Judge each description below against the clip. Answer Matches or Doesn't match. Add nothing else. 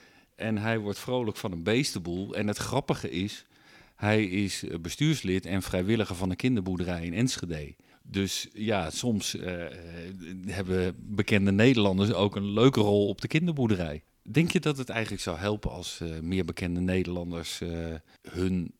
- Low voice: Matches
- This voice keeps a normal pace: Matches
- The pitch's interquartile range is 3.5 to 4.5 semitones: Matches